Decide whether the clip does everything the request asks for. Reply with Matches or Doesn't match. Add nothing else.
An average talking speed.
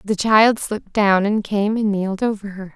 Doesn't match